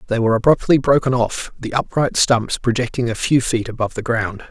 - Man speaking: Yes, male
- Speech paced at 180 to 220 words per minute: Yes, average, 200 wpm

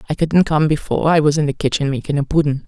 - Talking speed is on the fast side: Yes, fast, 245 wpm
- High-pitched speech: No, medium, 150 Hz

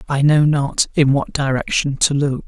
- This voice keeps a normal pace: Yes, average, 195 wpm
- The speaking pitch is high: No, medium, 140 Hz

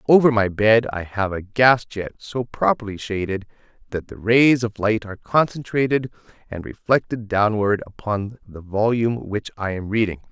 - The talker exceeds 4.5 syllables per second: Yes, 4.8 syllables/s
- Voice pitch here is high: No, low, 110 Hz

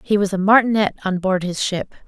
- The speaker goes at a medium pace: No, fast, 230 wpm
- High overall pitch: Yes, high, 195 Hz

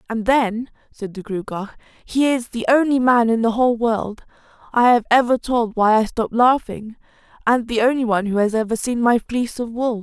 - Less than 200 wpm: No, fast, 205 wpm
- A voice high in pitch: Yes, high, 230 Hz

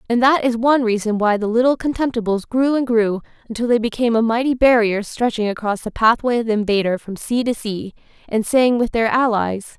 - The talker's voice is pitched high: Yes, high, 230 Hz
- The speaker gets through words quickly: Yes, fast, 210 wpm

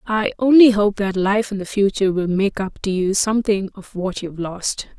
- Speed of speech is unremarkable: No, fast, 230 wpm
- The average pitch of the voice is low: No, high, 200 Hz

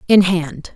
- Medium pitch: Yes, medium, 170 Hz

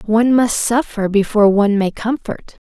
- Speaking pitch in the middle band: No, high, 220 Hz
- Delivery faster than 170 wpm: No, average, 155 wpm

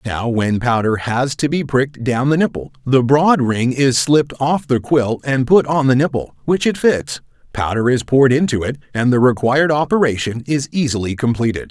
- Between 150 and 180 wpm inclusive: No, average, 195 wpm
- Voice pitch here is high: No, low, 130 Hz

